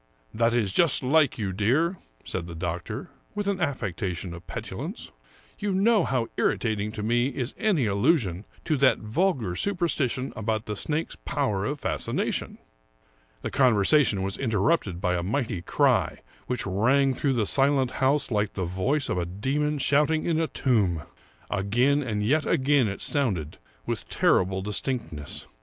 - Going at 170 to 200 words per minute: No, average, 155 wpm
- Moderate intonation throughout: No, wide, 6.6 semitones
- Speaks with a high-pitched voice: No, low, 120 Hz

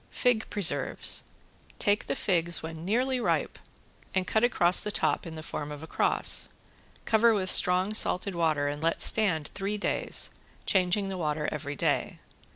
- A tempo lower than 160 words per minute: No, average, 165 wpm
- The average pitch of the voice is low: No, medium, 180 Hz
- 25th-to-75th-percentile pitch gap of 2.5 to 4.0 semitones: No, average, 4.7 semitones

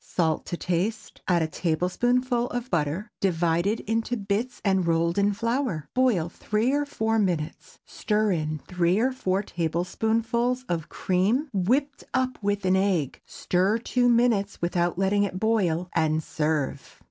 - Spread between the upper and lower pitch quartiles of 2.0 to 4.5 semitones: No, average, 5.1 semitones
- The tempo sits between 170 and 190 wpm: No, average, 145 wpm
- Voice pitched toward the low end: No, high, 195 Hz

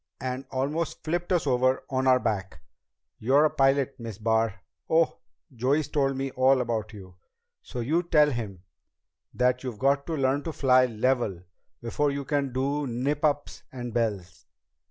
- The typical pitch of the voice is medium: No, low, 130 Hz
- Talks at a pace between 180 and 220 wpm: No, average, 160 wpm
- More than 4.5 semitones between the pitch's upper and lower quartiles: No, average, 3.4 semitones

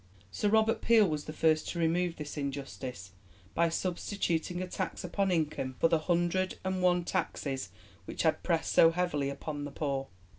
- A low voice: No, medium, 165 Hz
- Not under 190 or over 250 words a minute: No, average, 175 wpm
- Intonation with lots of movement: No, average, 3.8 semitones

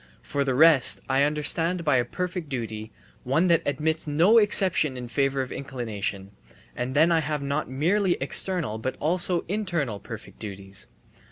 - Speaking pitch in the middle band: Yes, medium, 145 Hz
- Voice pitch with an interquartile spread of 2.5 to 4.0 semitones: No, average, 5.1 semitones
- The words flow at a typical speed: Yes, average, 160 wpm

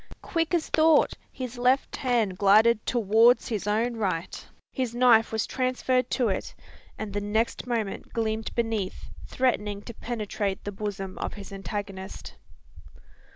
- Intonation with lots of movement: No, average, 3.2 semitones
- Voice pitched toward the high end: Yes, high, 220 Hz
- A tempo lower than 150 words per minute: Yes, average, 140 wpm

